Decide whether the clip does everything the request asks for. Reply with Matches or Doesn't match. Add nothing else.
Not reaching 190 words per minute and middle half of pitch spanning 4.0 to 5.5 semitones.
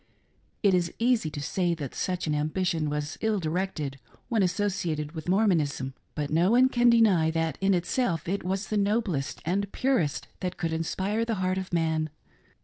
Matches